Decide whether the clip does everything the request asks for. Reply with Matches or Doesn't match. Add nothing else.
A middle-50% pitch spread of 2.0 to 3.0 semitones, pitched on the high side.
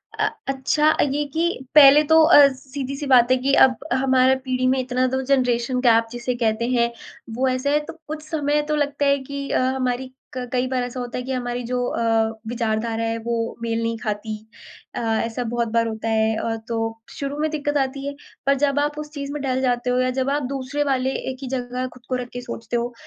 Matches